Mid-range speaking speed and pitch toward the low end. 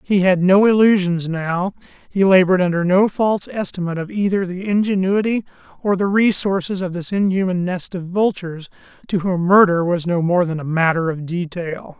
No: average, 175 wpm; medium, 185 Hz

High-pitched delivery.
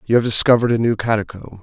No: low, 115 Hz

